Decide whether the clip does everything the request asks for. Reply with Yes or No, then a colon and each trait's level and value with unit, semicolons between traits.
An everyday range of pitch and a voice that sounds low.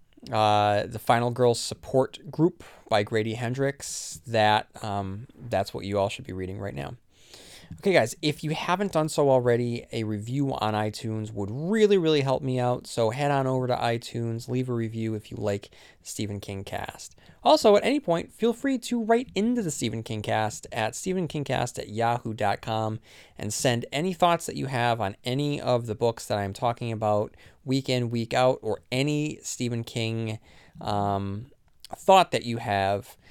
Yes: average, 4.6 semitones; low, 120 Hz